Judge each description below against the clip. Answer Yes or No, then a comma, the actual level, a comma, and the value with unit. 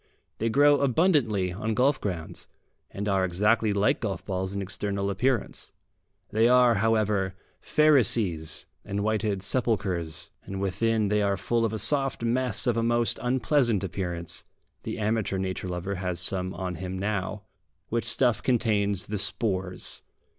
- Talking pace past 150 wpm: No, average, 145 wpm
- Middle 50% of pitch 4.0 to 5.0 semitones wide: No, average, 3.5 semitones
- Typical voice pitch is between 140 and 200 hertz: No, low, 105 Hz